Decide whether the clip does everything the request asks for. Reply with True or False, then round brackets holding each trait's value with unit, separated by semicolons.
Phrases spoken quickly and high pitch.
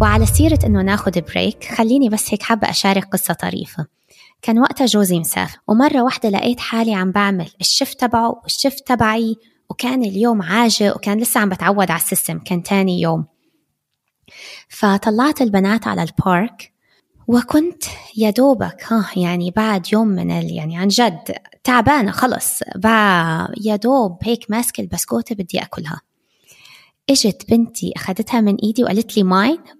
True (145 wpm; 215 Hz)